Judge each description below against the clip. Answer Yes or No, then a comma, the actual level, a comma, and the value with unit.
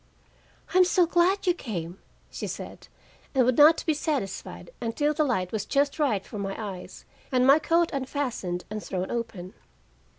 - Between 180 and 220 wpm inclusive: No, average, 165 wpm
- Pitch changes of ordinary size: No, wide, 7.5 semitones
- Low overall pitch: No, very high, 255 Hz